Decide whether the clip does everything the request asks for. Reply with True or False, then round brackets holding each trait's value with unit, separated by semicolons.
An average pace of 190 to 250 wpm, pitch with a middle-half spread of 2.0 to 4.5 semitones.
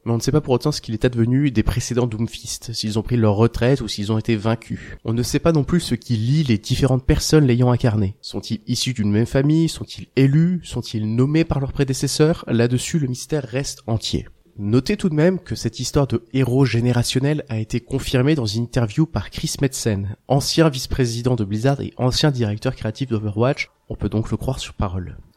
True (215 wpm; 3.6 semitones)